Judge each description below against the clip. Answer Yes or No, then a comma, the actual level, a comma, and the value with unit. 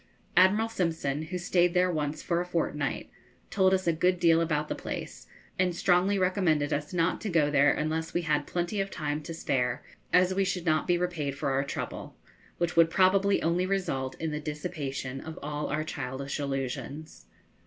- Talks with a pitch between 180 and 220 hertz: No, medium, 165 Hz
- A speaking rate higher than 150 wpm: Yes, average, 185 wpm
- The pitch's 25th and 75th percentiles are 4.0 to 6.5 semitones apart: No, average, 3.5 semitones